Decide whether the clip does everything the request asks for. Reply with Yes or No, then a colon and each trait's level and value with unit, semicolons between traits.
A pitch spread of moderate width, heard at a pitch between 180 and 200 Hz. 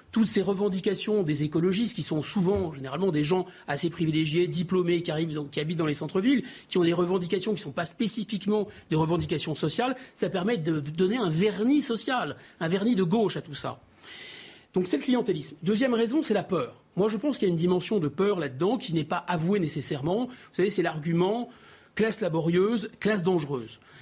Yes: average, 4.5 semitones; medium, 185 Hz